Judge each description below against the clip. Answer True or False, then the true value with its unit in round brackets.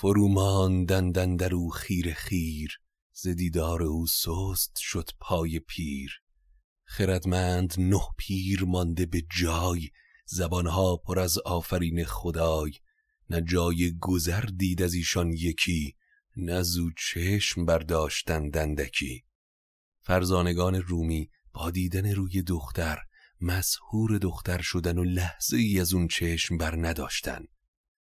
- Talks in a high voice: False (90 Hz)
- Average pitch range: False (1.9 semitones)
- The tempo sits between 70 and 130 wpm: True (110 wpm)